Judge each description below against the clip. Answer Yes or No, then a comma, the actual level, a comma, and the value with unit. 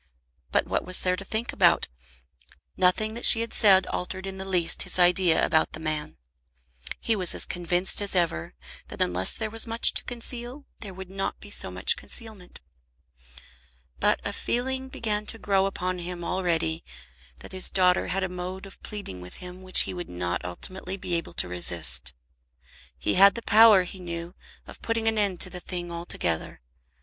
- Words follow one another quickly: No, average, 185 wpm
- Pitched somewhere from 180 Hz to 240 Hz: Yes, medium, 185 Hz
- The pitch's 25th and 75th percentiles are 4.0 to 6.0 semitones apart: No, average, 3.4 semitones